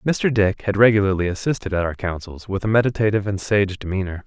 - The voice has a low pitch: Yes, low, 100 Hz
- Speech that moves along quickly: No, average, 195 wpm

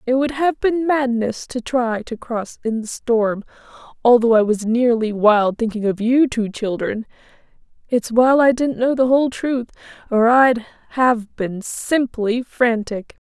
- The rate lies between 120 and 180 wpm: Yes, average, 165 wpm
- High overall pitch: Yes, high, 240 Hz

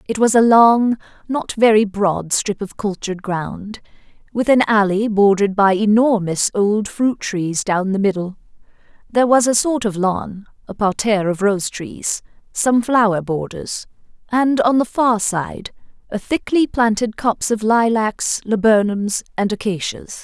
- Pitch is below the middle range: No, high, 210 Hz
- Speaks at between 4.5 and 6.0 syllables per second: No, 4.3 syllables/s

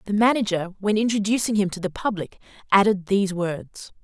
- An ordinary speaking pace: Yes, average, 165 wpm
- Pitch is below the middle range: No, high, 200 Hz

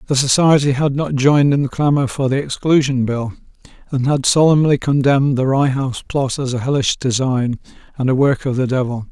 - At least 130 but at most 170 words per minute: No, average, 200 wpm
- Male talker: Yes, male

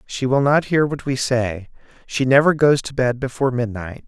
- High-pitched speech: No, low, 130 Hz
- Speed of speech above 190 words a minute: Yes, fast, 205 wpm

